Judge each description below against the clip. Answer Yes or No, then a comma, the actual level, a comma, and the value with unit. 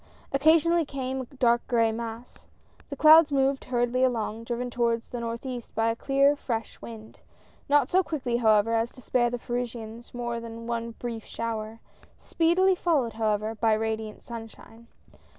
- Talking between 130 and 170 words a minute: Yes, average, 160 wpm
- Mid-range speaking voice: No, high, 235 Hz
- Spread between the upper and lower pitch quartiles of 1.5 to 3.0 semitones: Yes, average, 2.7 semitones